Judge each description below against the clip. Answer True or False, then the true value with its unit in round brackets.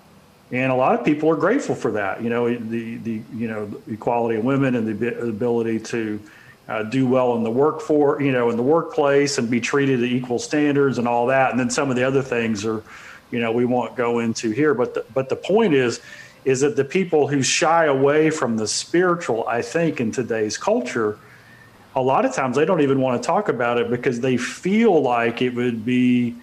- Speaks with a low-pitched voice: True (125 Hz)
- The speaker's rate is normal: False (225 wpm)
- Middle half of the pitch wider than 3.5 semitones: False (3.2 semitones)